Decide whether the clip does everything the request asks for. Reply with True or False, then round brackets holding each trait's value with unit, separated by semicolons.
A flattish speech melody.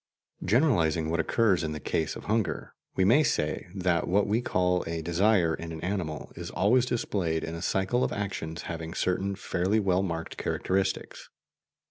False (3.7 semitones)